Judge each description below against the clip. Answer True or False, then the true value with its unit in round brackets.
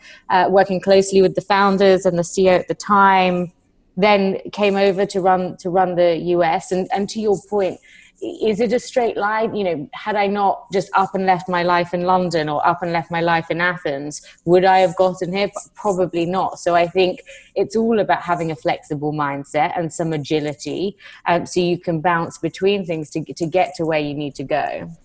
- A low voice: False (180 Hz)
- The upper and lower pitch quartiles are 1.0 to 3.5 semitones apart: True (2.6 semitones)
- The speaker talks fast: True (215 wpm)